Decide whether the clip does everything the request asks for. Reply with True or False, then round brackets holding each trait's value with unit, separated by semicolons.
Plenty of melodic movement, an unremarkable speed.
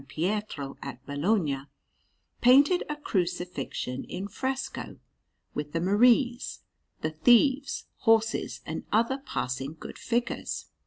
False (8.4 semitones; 105 wpm)